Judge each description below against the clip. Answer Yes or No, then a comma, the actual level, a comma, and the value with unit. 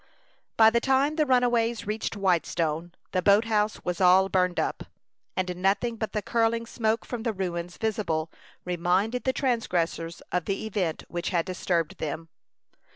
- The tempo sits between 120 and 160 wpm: Yes, average, 155 wpm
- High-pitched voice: Yes, high, 195 Hz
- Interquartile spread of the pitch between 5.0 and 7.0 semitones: No, average, 4.4 semitones